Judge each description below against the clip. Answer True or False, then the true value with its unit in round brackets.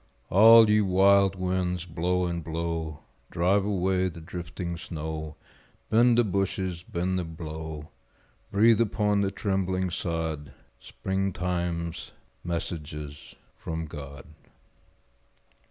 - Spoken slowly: True (105 wpm)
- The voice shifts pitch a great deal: False (2.9 semitones)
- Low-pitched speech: True (90 Hz)